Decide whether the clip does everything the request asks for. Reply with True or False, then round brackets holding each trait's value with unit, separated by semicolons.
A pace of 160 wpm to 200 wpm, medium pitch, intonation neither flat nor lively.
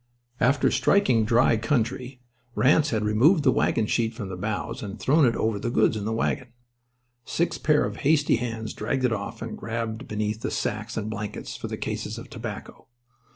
False (190 wpm; 115 Hz; 3.1 semitones)